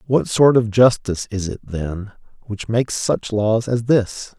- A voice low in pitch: Yes, low, 110 Hz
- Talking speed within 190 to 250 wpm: No, average, 180 wpm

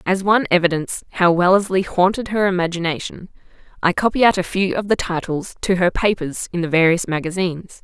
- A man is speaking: No, female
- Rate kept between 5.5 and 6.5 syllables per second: Yes, 5.9 syllables/s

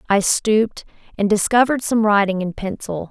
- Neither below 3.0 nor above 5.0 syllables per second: No, 5.4 syllables/s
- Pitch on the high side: Yes, high, 210 Hz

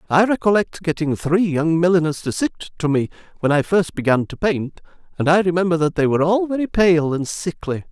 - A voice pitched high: No, medium, 165 Hz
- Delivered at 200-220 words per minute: Yes, fast, 205 wpm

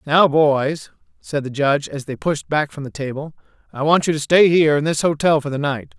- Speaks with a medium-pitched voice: Yes, medium, 150 Hz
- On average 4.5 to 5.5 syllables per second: Yes, 5.4 syllables/s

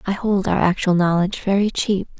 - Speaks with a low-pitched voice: No, high, 190 Hz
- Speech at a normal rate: Yes, average, 190 wpm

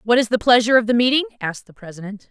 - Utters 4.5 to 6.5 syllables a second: No, 7.4 syllables/s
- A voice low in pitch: No, high, 230 Hz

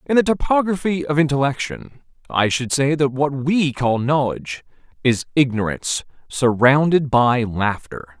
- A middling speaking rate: No, slow, 130 wpm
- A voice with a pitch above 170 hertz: No, low, 135 Hz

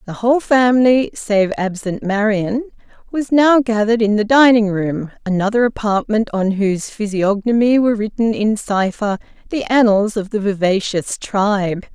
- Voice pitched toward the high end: Yes, high, 215 Hz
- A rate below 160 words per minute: Yes, average, 140 wpm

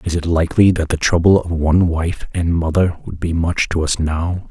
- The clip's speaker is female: No, male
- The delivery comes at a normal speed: No, fast, 225 wpm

